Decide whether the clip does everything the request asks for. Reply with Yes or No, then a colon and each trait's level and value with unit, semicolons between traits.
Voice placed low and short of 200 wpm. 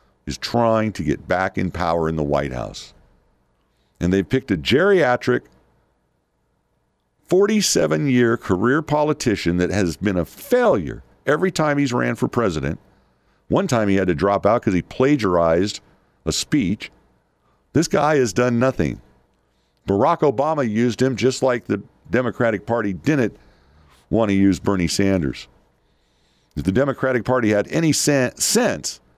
Yes: very low, 95 Hz; average, 145 wpm